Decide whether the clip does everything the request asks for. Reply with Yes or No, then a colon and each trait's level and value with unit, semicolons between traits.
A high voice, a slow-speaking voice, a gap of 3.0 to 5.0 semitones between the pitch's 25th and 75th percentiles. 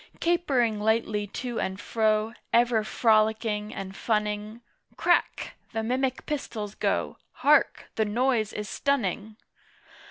No: high, 220 Hz; slow, 115 wpm; narrow, 2.4 semitones